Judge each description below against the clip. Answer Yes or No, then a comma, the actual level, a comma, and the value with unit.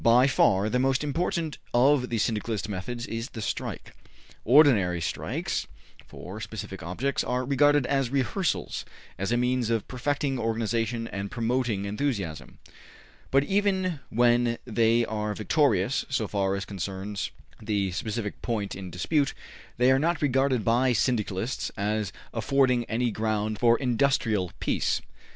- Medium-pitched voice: No, low, 115 Hz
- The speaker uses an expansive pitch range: No, average, 4.0 semitones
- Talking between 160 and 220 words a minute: No, slow, 135 wpm